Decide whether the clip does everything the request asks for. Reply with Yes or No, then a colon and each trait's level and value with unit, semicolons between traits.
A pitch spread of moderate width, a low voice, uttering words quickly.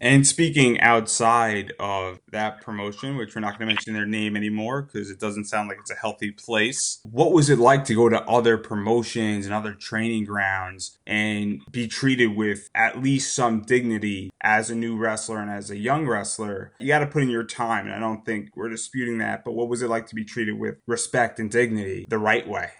No: narrow, 2.1 semitones; low, 110 Hz; fast, 220 wpm